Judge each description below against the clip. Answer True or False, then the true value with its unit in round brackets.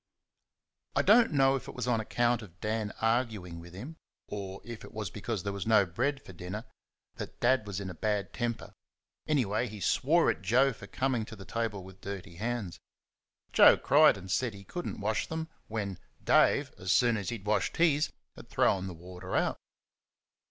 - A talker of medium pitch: False (110 Hz)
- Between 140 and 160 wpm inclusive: False (200 wpm)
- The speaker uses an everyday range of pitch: True (4.1 semitones)